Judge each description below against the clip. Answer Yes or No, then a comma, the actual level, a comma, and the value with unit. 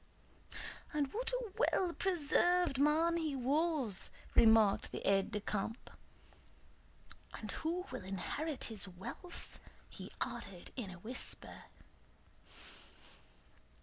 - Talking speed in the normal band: No, slow, 105 wpm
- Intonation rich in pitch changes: Yes, wide, 8.2 semitones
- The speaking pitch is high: Yes, very high, 280 Hz